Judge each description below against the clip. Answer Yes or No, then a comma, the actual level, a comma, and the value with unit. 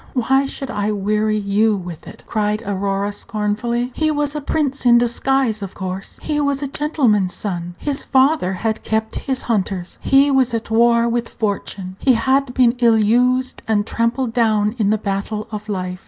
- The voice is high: Yes, high, 225 Hz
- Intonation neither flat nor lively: Yes, average, 4.0 semitones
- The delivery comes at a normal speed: Yes, average, 180 wpm